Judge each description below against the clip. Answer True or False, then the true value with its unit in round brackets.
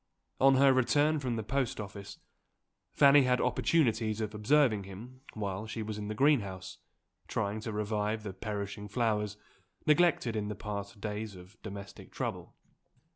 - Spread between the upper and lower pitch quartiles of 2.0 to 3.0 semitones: False (3.7 semitones)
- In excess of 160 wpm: False (150 wpm)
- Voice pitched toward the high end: False (110 Hz)